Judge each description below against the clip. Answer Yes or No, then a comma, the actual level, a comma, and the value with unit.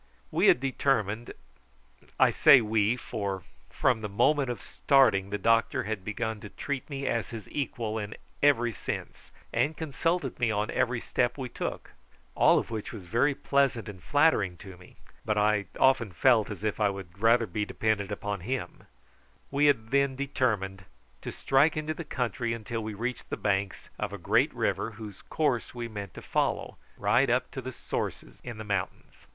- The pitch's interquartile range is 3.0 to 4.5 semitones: Yes, average, 4.2 semitones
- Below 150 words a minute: No, average, 180 wpm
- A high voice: No, low, 115 Hz